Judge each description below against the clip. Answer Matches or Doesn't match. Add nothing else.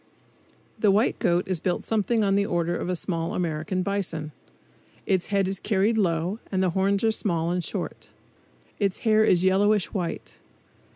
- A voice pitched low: Doesn't match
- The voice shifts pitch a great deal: Doesn't match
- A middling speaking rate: Matches